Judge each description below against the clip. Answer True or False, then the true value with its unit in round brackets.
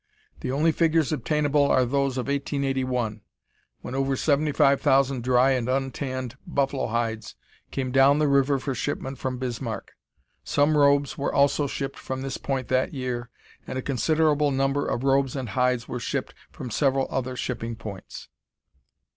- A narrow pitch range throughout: True (1.9 semitones)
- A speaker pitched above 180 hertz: False (135 Hz)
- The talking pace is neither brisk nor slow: True (160 wpm)